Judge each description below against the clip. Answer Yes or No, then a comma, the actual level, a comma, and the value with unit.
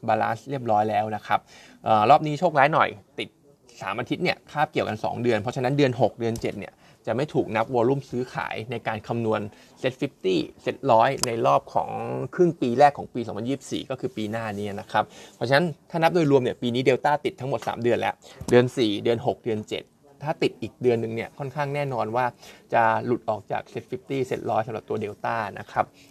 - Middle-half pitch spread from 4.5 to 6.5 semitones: No, average, 4.1 semitones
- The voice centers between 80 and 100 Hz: No, low, 120 Hz